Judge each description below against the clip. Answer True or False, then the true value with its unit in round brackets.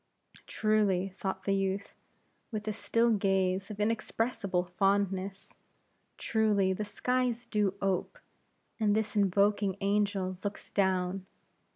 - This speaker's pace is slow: True (110 wpm)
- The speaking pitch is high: True (200 Hz)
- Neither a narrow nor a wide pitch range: False (2.0 semitones)